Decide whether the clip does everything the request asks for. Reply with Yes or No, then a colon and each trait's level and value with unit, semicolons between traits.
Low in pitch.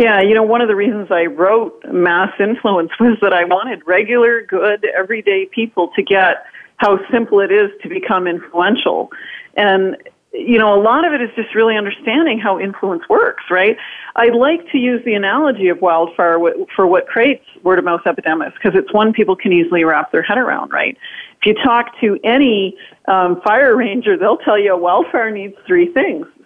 No: high, 210 Hz